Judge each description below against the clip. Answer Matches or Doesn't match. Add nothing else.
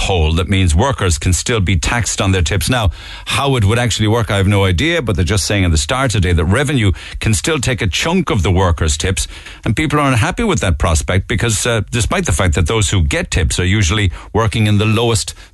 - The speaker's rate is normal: Doesn't match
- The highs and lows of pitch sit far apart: Doesn't match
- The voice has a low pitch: Matches